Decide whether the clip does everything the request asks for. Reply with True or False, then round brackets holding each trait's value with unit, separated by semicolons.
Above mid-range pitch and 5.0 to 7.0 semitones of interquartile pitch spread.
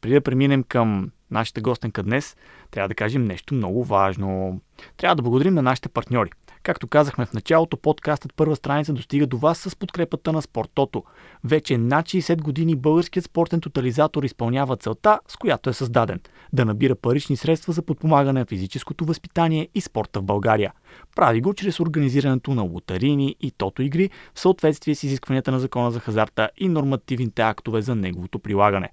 False (135 Hz; 5.3 semitones)